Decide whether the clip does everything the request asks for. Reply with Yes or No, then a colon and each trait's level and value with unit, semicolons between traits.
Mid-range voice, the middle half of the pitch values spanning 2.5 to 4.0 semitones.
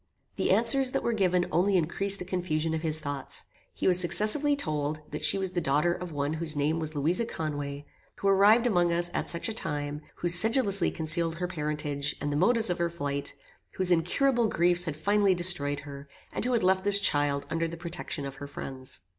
No: medium, 170 Hz; average, 4.4 semitones